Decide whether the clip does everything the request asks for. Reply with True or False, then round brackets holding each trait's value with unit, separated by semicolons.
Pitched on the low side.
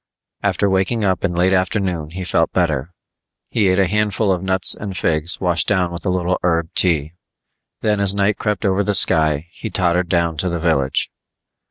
True (90 Hz)